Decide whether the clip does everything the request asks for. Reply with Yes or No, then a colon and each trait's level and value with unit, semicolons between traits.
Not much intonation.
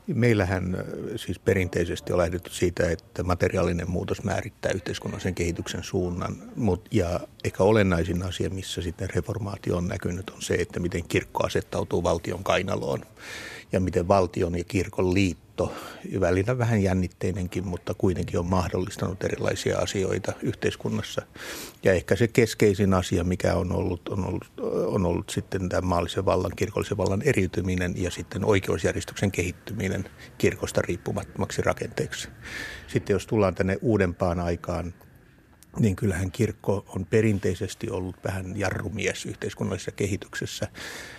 Yes: narrow, 2.3 semitones